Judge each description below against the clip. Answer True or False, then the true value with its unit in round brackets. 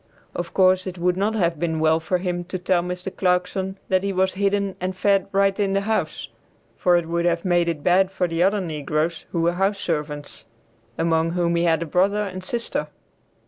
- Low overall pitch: False (180 Hz)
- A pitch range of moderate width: False (2.3 semitones)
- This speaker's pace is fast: True (210 wpm)